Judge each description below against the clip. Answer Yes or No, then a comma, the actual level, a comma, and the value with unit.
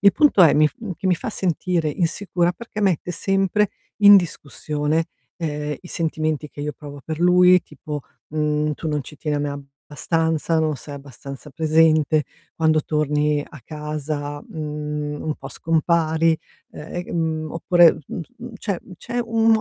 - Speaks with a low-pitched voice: No, medium, 155 Hz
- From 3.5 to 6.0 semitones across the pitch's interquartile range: No, average, 2.9 semitones